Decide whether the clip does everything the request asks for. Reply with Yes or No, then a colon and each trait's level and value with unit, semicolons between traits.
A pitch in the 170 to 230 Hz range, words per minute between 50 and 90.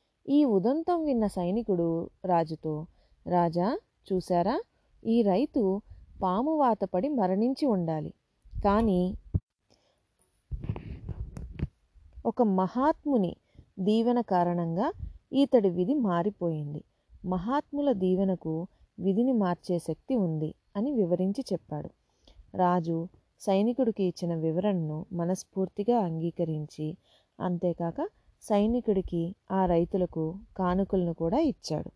Yes: high, 190 Hz; average, 80 wpm